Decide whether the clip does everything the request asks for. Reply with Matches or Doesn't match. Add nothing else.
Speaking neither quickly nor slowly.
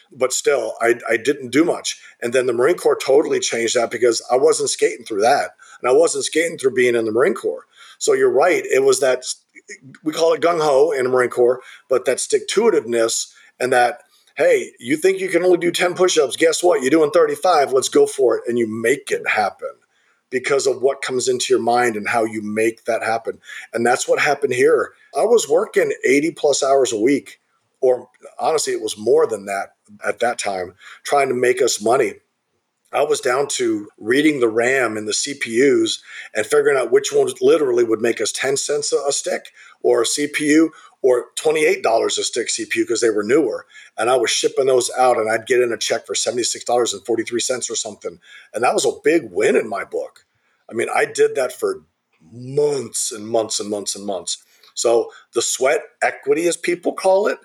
Doesn't match